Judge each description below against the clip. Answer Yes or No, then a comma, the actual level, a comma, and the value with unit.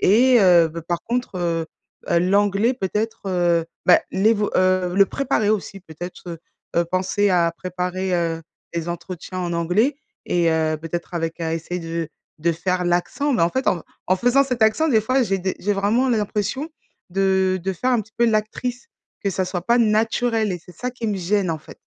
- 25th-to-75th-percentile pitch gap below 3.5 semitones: No, average, 4.2 semitones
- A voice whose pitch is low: No, high, 190 Hz